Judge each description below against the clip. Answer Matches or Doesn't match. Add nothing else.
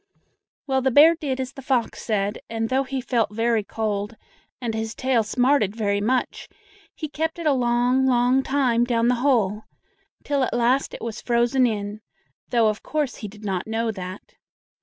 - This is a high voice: Matches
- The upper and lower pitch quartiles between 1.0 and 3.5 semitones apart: Matches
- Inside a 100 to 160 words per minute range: Doesn't match